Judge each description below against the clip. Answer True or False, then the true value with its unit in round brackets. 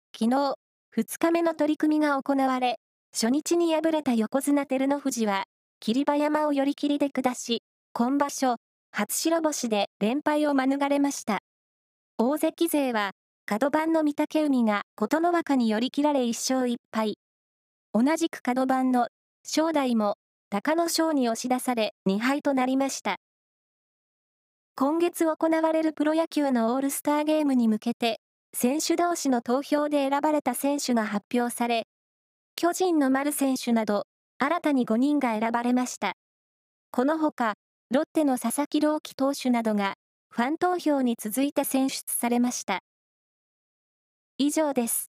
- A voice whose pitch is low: False (275 Hz)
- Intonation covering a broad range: False (4.1 semitones)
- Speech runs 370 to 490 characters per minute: False (265 characters per minute)